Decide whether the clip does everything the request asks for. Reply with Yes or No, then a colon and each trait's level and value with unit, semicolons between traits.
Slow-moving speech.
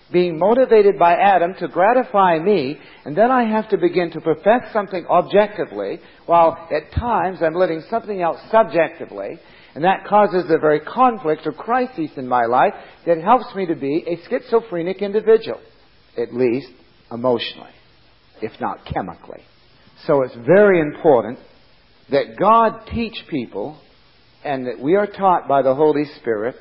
No: average, 150 wpm